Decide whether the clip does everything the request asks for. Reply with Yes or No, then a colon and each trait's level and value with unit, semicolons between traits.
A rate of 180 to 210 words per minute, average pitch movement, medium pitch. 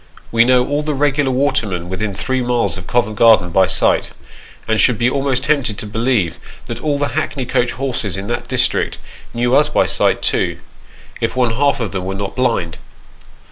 No: average, 190 wpm; average, 4.5 semitones; low, 120 Hz